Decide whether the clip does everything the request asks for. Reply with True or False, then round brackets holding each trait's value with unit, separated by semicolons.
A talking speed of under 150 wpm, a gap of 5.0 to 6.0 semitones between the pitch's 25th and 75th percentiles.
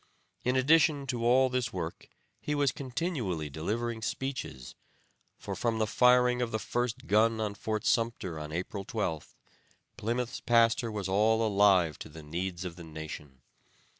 False (155 wpm; 5.5 semitones)